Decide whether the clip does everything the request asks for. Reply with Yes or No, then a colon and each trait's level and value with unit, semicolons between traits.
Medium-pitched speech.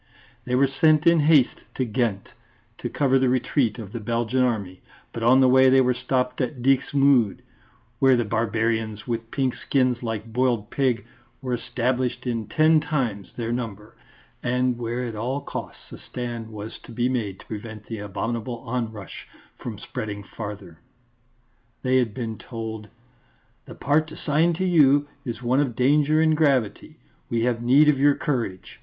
No: low, 125 Hz